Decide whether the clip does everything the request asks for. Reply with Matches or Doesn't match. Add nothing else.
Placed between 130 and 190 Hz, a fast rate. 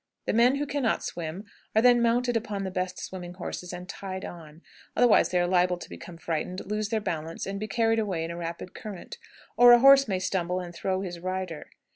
Matches